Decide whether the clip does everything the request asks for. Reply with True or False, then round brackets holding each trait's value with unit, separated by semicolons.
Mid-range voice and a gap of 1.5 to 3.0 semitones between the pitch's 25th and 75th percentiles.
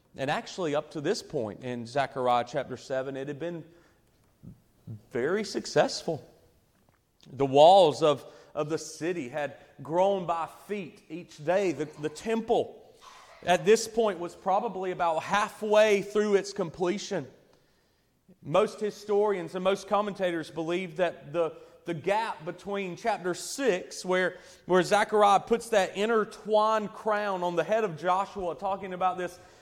False (180 Hz; 3.9 semitones)